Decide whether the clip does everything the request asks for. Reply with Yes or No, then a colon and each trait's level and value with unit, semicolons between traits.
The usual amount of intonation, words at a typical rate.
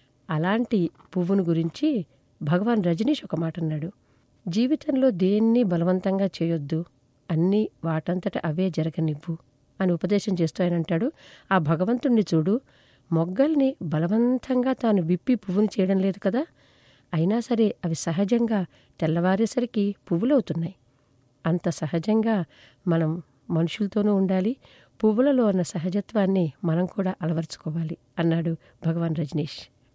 Yes: average, 4.5 semitones; average, 100 wpm